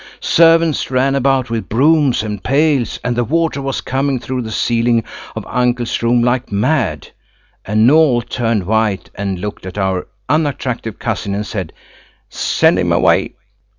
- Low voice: Yes, low, 120 Hz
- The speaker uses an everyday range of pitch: Yes, average, 4.1 semitones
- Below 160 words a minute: Yes, average, 150 wpm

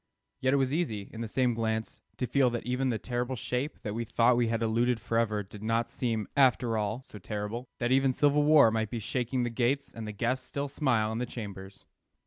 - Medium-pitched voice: No, low, 120 Hz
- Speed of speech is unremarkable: No, fast, 225 wpm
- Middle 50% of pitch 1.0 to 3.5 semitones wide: Yes, average, 2.7 semitones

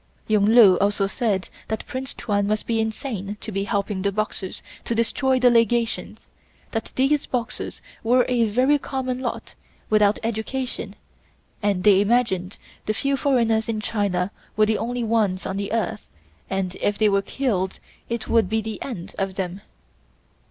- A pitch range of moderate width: Yes, average, 3.1 semitones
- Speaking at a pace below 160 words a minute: No, average, 165 wpm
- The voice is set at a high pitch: Yes, high, 220 Hz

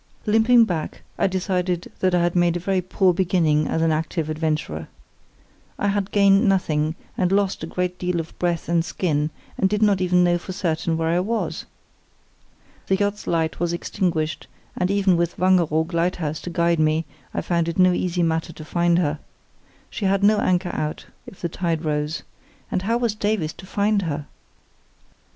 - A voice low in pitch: No, medium, 175 Hz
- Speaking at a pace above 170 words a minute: Yes, average, 180 wpm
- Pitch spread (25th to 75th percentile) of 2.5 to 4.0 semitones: Yes, average, 2.8 semitones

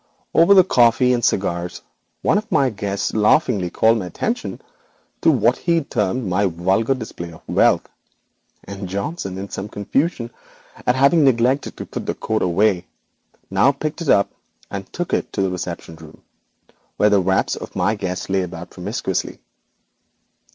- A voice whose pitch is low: Yes, low, 105 Hz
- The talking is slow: No, average, 160 wpm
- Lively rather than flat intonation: Yes, wide, 5.8 semitones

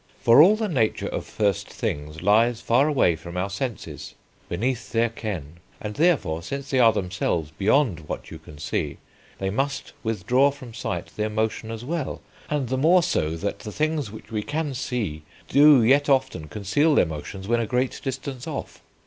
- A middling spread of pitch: No, wide, 6.1 semitones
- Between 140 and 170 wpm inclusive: No, average, 185 wpm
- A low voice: Yes, low, 115 Hz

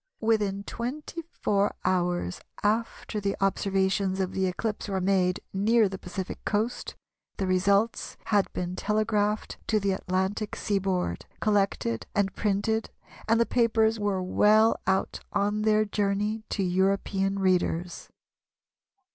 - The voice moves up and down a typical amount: No, narrow, 2.2 semitones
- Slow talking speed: Yes, slow, 125 wpm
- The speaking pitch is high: Yes, high, 200 Hz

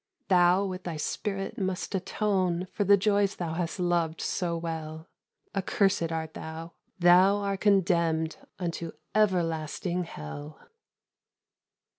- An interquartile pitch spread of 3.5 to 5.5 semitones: No, average, 2.9 semitones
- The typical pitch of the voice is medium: Yes, medium, 175 Hz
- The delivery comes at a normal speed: No, slow, 115 wpm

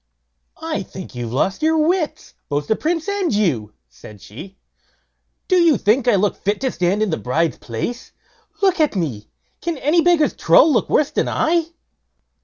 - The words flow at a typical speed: Yes, average, 175 wpm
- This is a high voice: Yes, high, 225 Hz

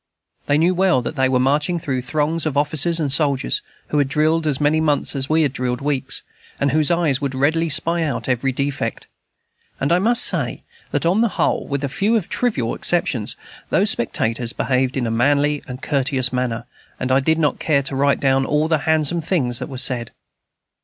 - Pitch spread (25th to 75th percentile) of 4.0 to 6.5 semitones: No, average, 3.3 semitones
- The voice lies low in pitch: No, medium, 145 Hz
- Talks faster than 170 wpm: Yes, average, 200 wpm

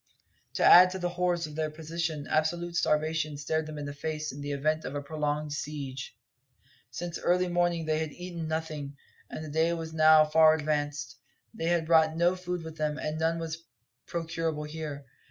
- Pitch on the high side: No, medium, 160 Hz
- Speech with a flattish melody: Yes, narrow, 1.7 semitones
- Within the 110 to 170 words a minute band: No, average, 190 wpm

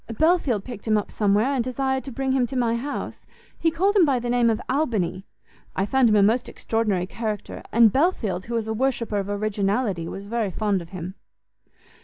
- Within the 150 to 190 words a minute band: No, fast, 205 wpm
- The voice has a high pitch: Yes, high, 230 Hz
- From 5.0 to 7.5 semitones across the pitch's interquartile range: No, average, 4.4 semitones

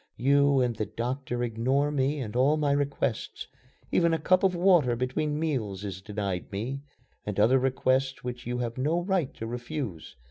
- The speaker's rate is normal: Yes, average, 175 wpm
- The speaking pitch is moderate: No, low, 130 Hz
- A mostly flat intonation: No, average, 3.9 semitones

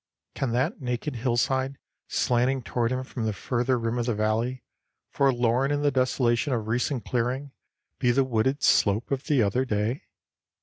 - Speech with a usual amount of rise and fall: No, narrow, 2.2 semitones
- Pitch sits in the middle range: No, low, 125 Hz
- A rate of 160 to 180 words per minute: Yes, average, 165 wpm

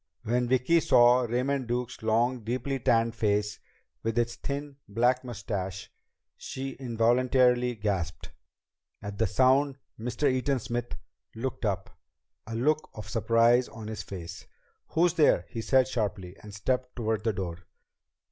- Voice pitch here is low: Yes, low, 120 Hz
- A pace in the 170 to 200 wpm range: No, average, 140 wpm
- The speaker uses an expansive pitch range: No, average, 3.1 semitones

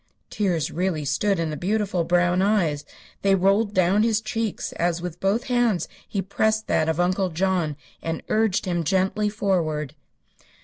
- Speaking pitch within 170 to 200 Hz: Yes, medium, 185 Hz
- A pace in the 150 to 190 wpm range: Yes, average, 160 wpm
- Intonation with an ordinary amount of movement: Yes, average, 3.7 semitones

